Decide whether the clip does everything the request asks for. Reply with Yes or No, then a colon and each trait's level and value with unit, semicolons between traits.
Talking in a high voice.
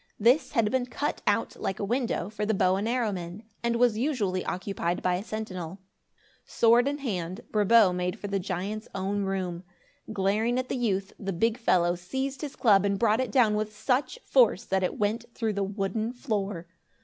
Yes: high, 210 Hz